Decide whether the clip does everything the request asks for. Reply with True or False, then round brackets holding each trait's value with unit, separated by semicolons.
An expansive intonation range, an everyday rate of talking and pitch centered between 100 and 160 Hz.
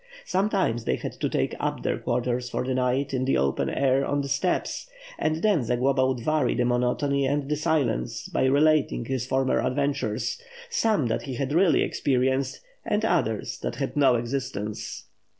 False (2.8 semitones; 175 wpm; 135 Hz)